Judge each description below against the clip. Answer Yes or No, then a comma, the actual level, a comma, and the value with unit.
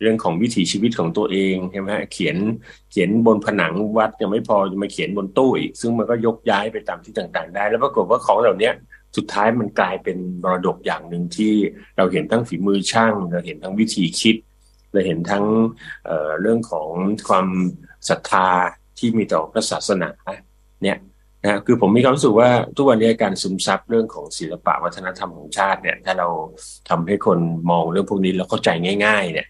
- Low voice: Yes, low, 105 Hz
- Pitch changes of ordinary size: Yes, average, 3.5 semitones